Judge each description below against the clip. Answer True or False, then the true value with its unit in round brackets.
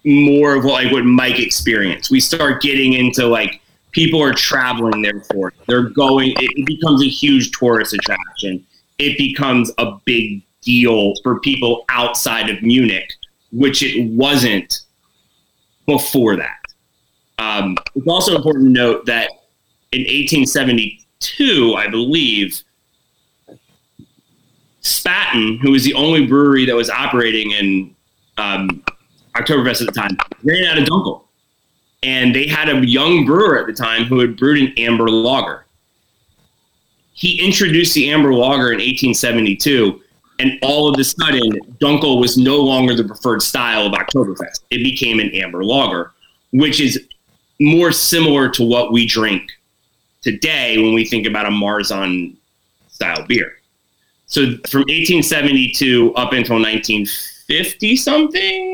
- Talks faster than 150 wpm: False (135 wpm)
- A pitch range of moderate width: True (3.7 semitones)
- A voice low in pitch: True (125 Hz)